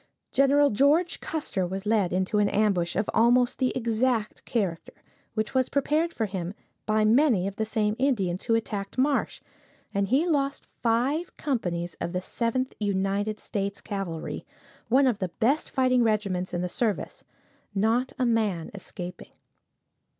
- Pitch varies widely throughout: No, average, 4.8 semitones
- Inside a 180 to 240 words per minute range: No, average, 150 wpm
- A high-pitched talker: Yes, high, 220 Hz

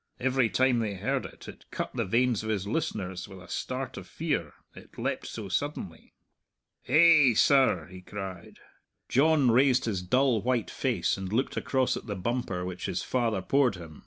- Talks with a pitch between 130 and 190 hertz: No, low, 115 Hz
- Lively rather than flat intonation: Yes, wide, 5.8 semitones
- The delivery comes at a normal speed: Yes, average, 180 wpm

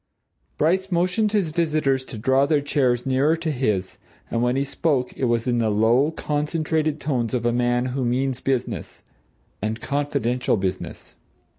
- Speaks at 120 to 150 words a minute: No, average, 160 wpm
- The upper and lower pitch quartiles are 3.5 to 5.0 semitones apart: Yes, average, 4.1 semitones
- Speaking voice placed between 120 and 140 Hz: Yes, low, 135 Hz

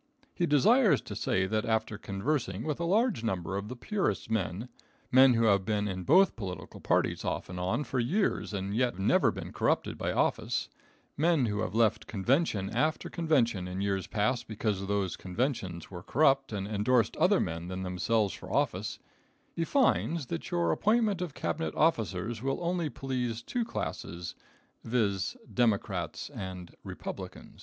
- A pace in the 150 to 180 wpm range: Yes, average, 165 wpm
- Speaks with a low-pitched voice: Yes, low, 115 Hz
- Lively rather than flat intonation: Yes, wide, 6.8 semitones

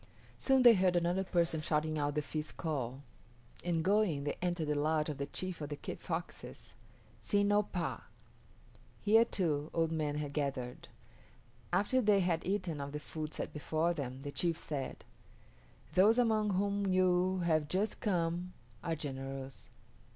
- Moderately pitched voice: Yes, medium, 165 Hz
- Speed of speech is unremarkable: Yes, average, 160 wpm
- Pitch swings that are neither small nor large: Yes, average, 4.1 semitones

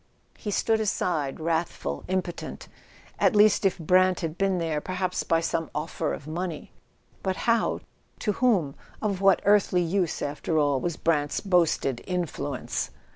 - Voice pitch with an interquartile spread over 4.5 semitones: No, average, 3.6 semitones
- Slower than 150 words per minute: Yes, average, 140 wpm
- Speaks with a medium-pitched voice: Yes, medium, 175 Hz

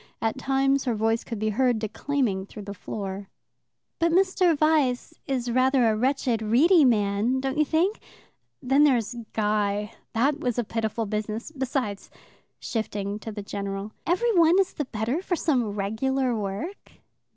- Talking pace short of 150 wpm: No, average, 160 wpm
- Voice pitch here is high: Yes, high, 240 Hz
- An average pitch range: Yes, average, 4.8 semitones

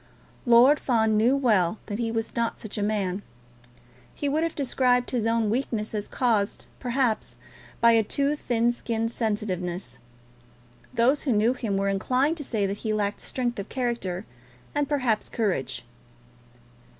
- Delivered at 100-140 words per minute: No, average, 155 wpm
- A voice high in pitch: Yes, high, 230 Hz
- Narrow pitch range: No, average, 3.3 semitones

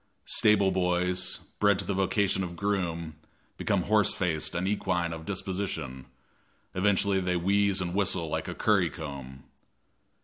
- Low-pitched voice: Yes, very low, 90 Hz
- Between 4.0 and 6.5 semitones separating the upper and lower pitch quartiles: No, average, 2.8 semitones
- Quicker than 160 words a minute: No, average, 140 wpm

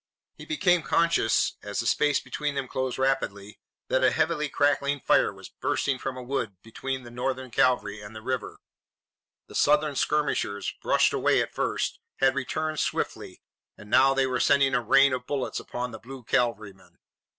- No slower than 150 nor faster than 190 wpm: Yes, average, 175 wpm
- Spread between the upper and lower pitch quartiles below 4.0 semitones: Yes, average, 3.2 semitones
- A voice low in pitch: Yes, low, 130 Hz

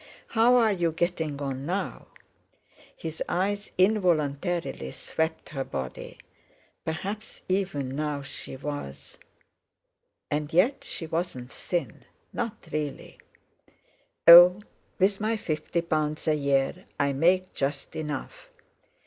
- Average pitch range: Yes, average, 4.6 semitones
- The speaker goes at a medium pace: No, slow, 105 wpm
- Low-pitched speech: No, medium, 160 Hz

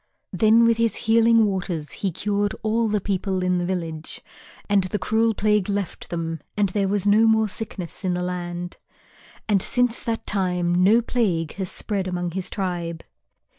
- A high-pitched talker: Yes, high, 195 Hz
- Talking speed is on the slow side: No, average, 170 wpm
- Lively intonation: No, average, 3.4 semitones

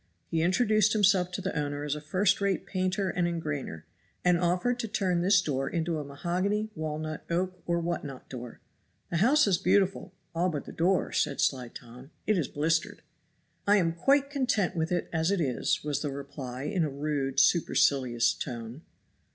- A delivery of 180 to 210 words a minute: Yes, average, 185 wpm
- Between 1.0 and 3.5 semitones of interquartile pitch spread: No, average, 4.8 semitones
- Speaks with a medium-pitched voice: Yes, medium, 170 Hz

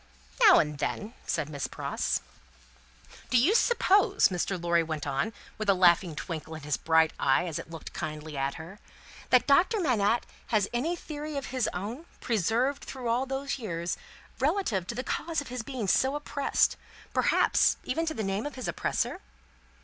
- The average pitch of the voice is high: Yes, high, 220 Hz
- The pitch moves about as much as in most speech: No, wide, 8.6 semitones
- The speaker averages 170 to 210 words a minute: Yes, average, 175 wpm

